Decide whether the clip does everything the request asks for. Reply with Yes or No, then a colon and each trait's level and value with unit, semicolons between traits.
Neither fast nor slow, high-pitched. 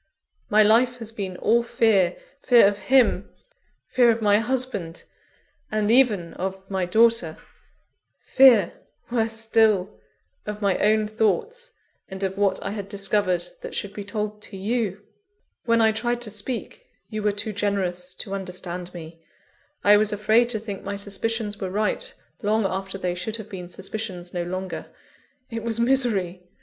Yes: average, 160 wpm; high, 210 Hz